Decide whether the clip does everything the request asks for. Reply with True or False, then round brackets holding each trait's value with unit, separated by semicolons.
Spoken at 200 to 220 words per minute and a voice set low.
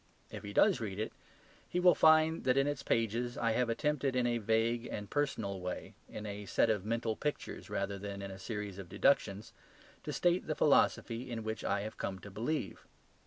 True (205 wpm; 115 Hz)